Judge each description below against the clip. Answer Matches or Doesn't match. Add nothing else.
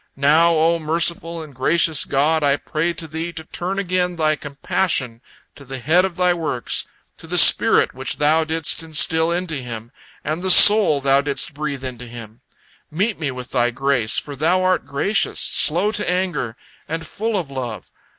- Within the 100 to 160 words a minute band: Doesn't match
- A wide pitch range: Doesn't match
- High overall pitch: Doesn't match